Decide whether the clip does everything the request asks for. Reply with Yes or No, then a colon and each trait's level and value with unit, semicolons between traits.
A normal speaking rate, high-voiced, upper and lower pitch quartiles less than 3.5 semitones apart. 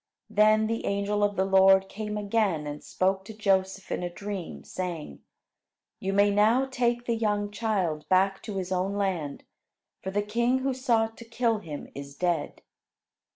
Yes: average, 170 wpm; high, 200 Hz; average, 2.7 semitones